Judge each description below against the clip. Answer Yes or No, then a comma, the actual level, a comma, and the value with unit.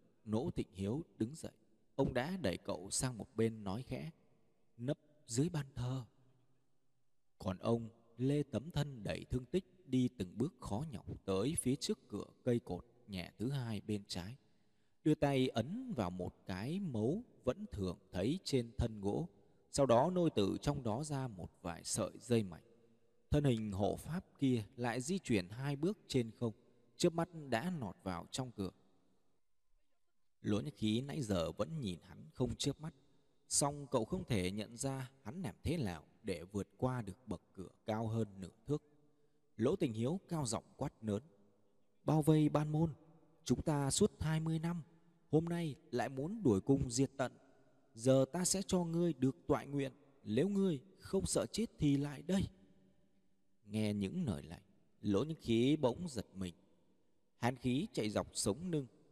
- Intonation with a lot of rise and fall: Yes, wide, 6.1 semitones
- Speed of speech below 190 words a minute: Yes, average, 175 wpm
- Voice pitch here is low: Yes, low, 125 Hz